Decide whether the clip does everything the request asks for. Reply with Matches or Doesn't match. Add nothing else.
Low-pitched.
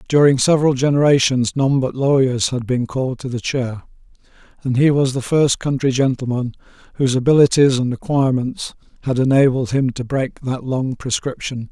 Matches